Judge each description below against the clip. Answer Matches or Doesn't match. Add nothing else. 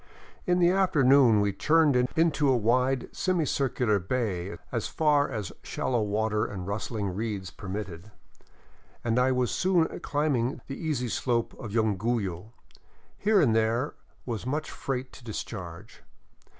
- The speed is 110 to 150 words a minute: Matches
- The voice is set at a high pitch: Doesn't match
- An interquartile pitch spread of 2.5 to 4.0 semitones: Doesn't match